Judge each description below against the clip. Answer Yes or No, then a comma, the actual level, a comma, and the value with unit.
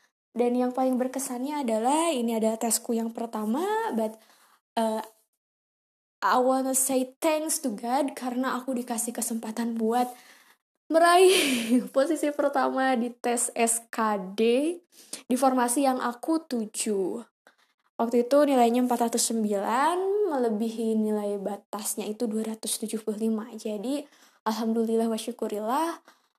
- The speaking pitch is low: No, high, 240 Hz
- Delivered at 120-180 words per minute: No, average, 105 wpm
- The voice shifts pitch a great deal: No, average, 3.0 semitones